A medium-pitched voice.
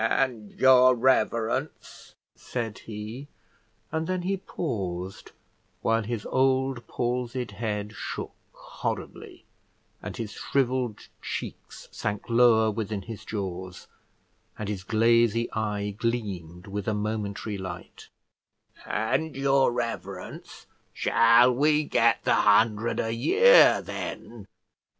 No: low, 115 Hz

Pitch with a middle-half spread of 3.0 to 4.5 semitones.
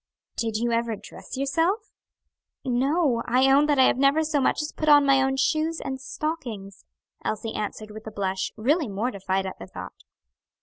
No: average, 5.2 semitones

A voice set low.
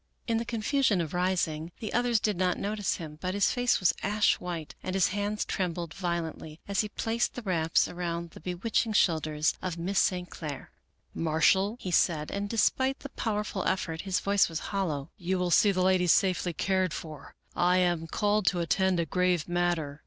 No: medium, 180 Hz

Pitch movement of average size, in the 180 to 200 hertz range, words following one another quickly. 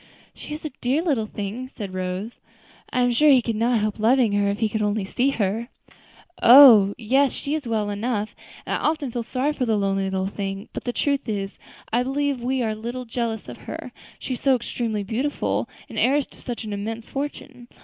No: average, 3.9 semitones; high, 235 Hz; fast, 215 wpm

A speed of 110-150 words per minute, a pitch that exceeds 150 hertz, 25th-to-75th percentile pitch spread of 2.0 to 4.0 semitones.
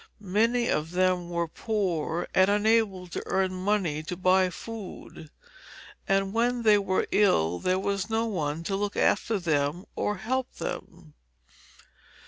Yes: average, 140 wpm; high, 190 Hz; average, 3.4 semitones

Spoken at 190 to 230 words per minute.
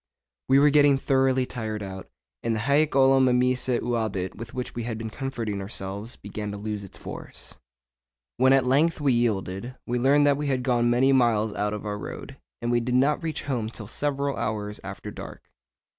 Yes: average, 195 wpm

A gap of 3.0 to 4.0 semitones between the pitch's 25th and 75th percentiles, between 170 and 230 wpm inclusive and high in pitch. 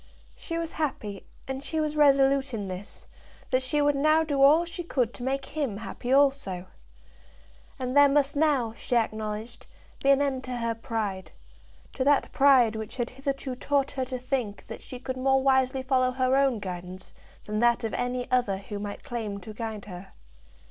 Yes: average, 3.7 semitones; average, 185 wpm; very high, 255 Hz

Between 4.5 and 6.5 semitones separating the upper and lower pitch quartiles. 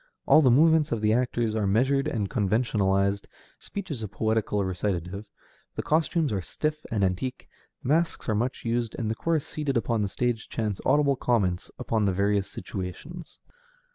Yes: average, 5.3 semitones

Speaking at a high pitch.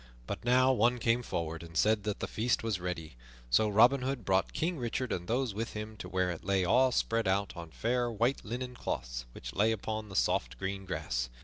No: low, 110 Hz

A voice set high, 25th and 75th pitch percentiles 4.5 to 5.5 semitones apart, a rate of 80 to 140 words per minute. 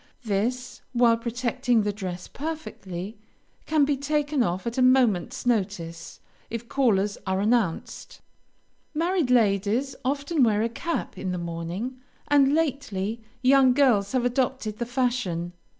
Yes: high, 240 Hz; average, 5.0 semitones; slow, 135 wpm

